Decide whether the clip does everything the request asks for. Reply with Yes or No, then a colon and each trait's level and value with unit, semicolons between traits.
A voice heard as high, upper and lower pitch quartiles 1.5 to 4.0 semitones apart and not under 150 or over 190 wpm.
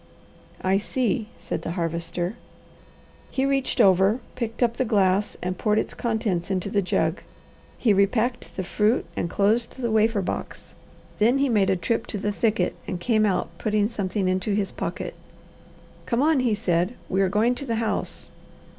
Yes: high, 210 Hz; average, 3.5 semitones; average, 170 wpm